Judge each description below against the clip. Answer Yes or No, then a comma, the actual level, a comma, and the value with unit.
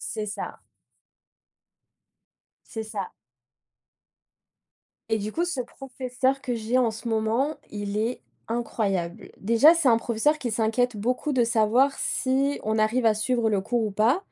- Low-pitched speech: No, high, 230 Hz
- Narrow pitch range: No, average, 3.0 semitones